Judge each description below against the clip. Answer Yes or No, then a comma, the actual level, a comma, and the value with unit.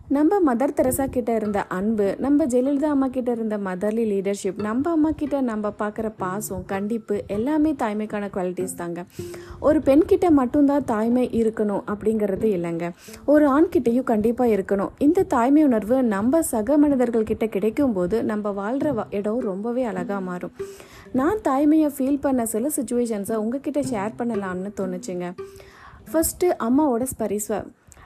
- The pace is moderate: No, fast, 135 wpm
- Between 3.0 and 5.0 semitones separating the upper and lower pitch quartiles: No, wide, 5.6 semitones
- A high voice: Yes, high, 230 Hz